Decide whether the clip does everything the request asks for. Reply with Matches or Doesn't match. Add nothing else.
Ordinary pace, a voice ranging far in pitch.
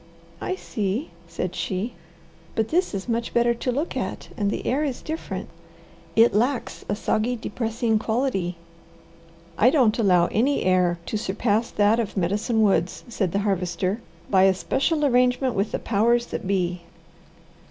Doesn't match